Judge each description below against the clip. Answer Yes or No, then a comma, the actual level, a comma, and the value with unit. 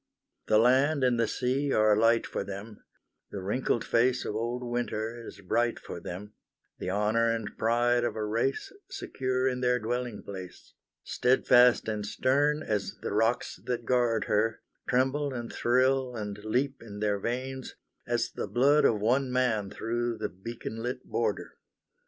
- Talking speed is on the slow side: No, average, 160 wpm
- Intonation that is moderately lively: Yes, average, 3.0 semitones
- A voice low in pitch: Yes, low, 120 Hz